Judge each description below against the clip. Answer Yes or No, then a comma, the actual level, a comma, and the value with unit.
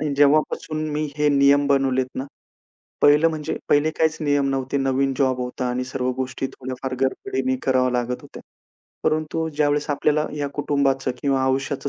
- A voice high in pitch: No, medium, 140 Hz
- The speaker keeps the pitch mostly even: Yes, narrow, 2.2 semitones